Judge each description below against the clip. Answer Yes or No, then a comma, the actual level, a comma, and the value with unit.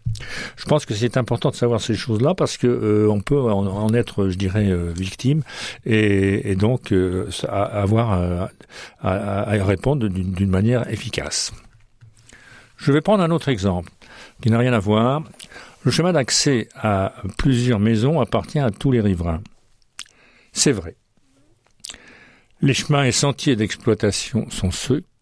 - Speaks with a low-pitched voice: Yes, low, 110 Hz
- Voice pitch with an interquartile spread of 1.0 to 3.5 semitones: No, average, 4.2 semitones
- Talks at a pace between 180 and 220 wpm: No, average, 150 wpm